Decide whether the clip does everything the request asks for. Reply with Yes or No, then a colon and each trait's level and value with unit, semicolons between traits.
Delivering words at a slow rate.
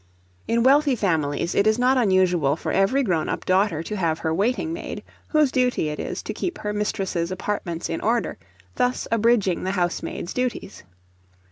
No: average, 170 wpm